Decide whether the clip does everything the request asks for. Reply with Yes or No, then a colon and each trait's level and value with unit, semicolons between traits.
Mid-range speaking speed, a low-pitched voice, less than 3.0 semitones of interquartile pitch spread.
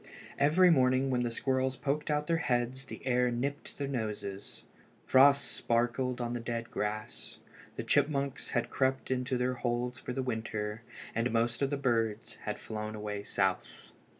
Yes: average, 165 wpm; low, 125 Hz; narrow, 2.6 semitones